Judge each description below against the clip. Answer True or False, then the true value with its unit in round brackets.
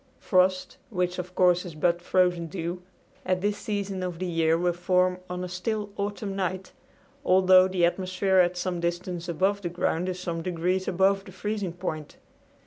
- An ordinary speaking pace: True (175 wpm)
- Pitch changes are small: True (1.4 semitones)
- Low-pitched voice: False (180 Hz)